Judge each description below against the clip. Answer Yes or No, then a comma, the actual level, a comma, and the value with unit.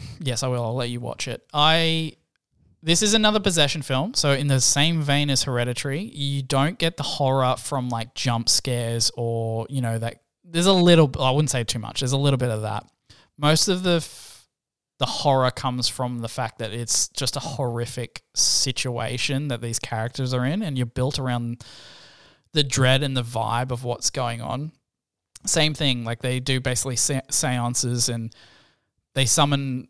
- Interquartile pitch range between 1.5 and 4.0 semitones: Yes, average, 3.1 semitones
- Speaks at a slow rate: No, average, 185 wpm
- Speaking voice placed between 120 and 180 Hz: Yes, low, 130 Hz